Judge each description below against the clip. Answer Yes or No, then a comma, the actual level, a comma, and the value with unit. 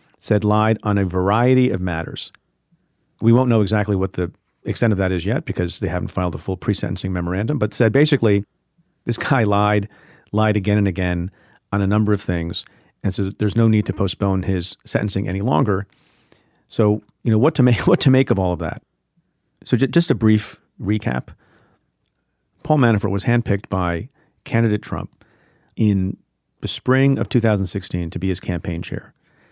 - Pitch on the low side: Yes, low, 105 Hz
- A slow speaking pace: No, average, 175 wpm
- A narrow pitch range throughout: No, average, 3.7 semitones